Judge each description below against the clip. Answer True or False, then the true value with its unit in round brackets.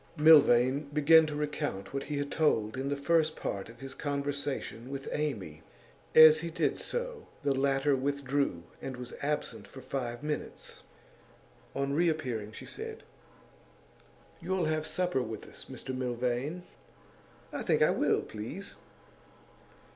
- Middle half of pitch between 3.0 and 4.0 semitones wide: True (3.6 semitones)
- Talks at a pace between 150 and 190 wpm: False (140 wpm)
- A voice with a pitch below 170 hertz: True (140 Hz)